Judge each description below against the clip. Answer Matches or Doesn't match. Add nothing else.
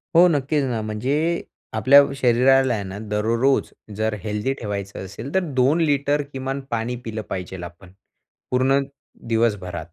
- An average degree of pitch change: Matches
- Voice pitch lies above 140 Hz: Doesn't match